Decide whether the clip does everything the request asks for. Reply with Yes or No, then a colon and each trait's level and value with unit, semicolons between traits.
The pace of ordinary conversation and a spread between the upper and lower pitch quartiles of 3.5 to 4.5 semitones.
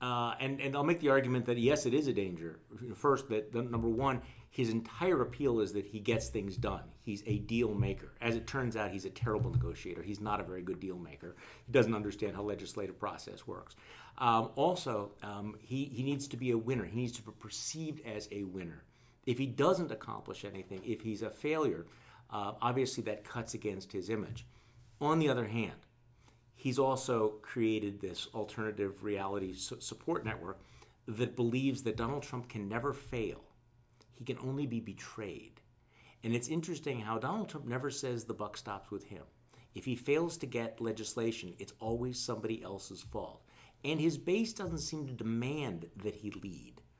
Yes: average, 185 wpm; average, 3.8 semitones